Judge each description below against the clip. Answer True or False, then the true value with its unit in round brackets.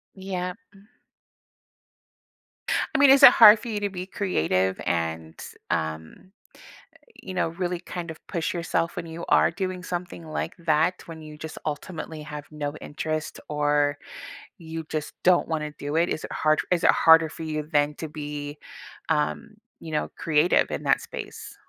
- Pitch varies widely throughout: False (3.3 semitones)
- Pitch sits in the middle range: True (160 Hz)